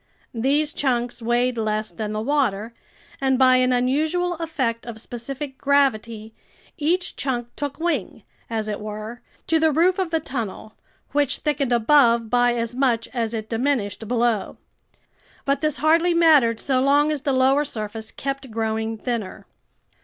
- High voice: Yes, very high, 250 Hz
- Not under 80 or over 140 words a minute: No, average, 155 wpm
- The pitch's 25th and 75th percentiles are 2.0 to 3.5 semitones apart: No, average, 4.2 semitones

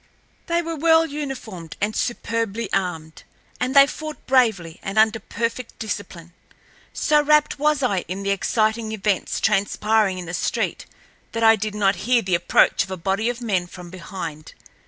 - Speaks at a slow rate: No, average, 165 wpm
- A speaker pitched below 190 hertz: No, high, 215 Hz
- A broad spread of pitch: No, average, 4.9 semitones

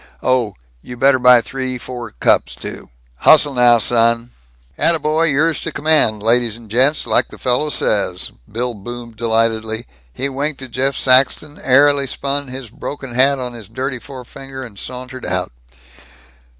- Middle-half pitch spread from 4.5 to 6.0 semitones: No, average, 2.8 semitones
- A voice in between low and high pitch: No, low, 125 Hz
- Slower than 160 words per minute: Yes, average, 150 wpm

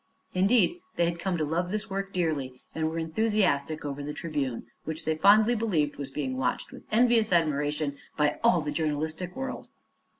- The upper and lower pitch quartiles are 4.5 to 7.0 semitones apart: Yes, average, 5.0 semitones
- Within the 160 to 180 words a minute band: Yes, average, 175 wpm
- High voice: No, medium, 160 Hz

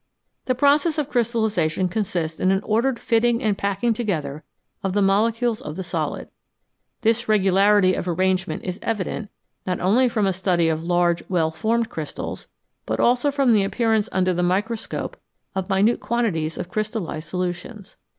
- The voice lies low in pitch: No, high, 200 Hz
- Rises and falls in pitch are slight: No, average, 4.1 semitones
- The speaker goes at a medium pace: Yes, average, 160 wpm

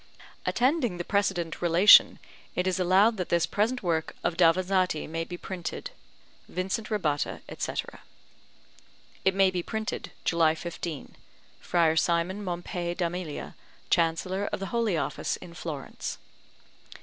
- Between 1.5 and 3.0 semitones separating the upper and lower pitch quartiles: Yes, narrow, 2.5 semitones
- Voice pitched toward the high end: No, medium, 180 Hz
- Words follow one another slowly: Yes, slow, 125 wpm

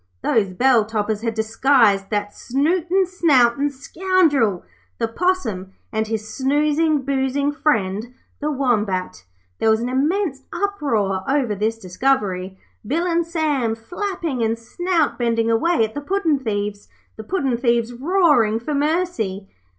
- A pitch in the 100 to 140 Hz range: No, very high, 250 Hz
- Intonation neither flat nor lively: No, wide, 5.8 semitones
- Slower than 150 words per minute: Yes, slow, 135 wpm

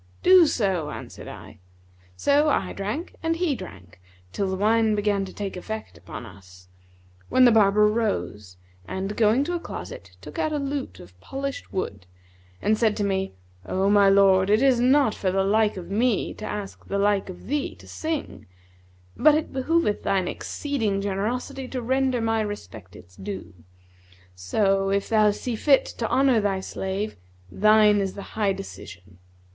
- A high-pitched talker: Yes, high, 210 Hz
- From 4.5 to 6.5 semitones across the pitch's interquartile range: Yes, average, 4.8 semitones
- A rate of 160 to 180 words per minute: Yes, average, 170 wpm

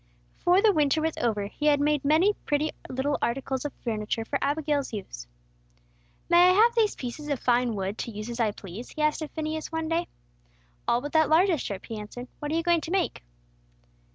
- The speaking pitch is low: No, very high, 290 Hz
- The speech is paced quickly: Yes, fast, 210 wpm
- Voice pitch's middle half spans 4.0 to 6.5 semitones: Yes, average, 5.2 semitones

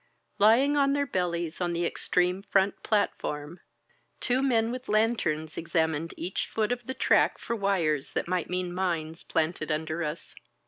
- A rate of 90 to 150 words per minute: No, average, 165 wpm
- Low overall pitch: No, medium, 180 Hz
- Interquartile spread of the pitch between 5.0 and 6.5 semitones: Yes, wide, 5.5 semitones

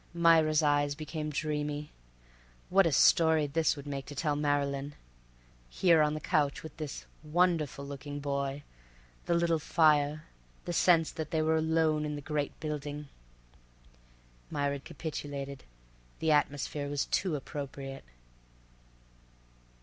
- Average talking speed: No, slow, 120 wpm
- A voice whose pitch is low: No, medium, 150 Hz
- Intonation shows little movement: Yes, narrow, 1.9 semitones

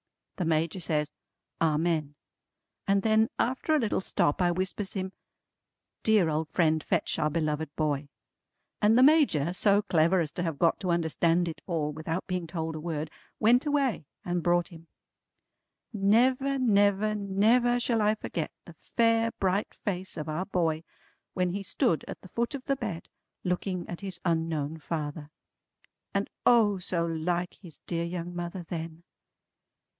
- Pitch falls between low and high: Yes, medium, 175 Hz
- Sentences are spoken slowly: No, average, 160 wpm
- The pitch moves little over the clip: No, average, 4.2 semitones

